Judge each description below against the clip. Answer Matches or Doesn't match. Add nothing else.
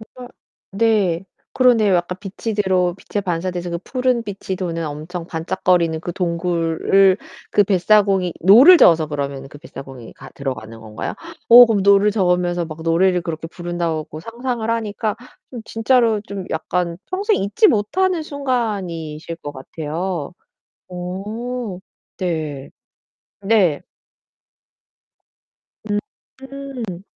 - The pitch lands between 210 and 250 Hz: Doesn't match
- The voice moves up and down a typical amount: Matches